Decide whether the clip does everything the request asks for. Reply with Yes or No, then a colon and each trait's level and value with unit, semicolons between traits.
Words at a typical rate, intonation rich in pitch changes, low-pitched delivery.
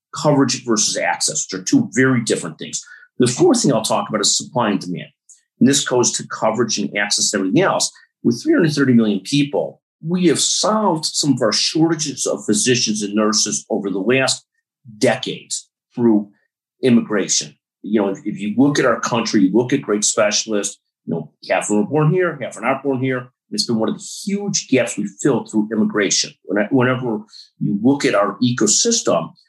Yes: average, 190 wpm; wide, 6.4 semitones; low, 125 Hz